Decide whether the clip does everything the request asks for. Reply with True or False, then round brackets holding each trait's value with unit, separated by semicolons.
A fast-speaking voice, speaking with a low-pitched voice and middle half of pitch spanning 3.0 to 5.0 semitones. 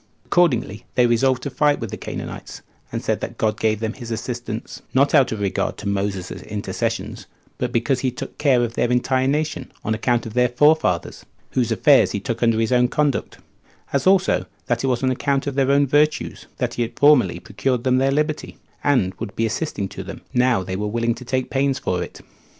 True (210 wpm; 125 Hz; 3.6 semitones)